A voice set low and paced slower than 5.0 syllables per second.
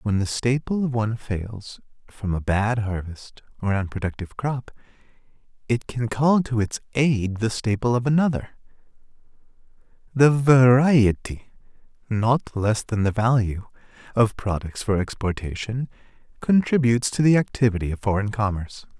Yes: low, 115 Hz; 4.8 syllables/s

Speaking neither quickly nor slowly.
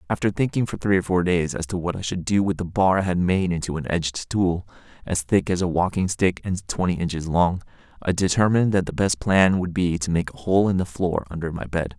No: fast, 255 wpm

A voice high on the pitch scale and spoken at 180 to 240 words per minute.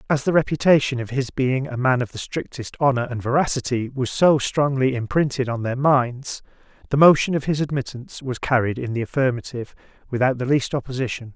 No: low, 130 Hz; average, 185 wpm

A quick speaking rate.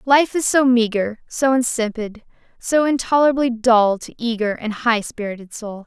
No: average, 155 wpm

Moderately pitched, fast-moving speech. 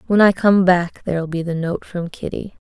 Yes: medium, 180 Hz; fast, 225 wpm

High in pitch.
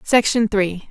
Yes: high, 210 Hz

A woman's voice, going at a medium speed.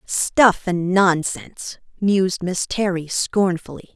No: female; slow, 105 wpm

